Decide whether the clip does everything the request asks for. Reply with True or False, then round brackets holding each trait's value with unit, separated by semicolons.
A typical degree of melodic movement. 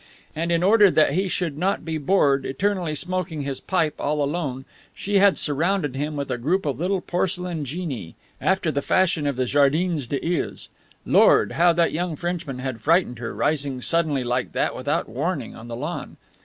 True (4.5 semitones)